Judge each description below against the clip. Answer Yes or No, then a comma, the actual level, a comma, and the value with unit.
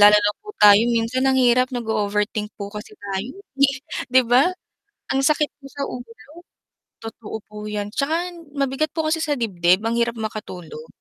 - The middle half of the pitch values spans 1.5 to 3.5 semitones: No, average, 4.3 semitones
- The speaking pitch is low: No, high, 230 Hz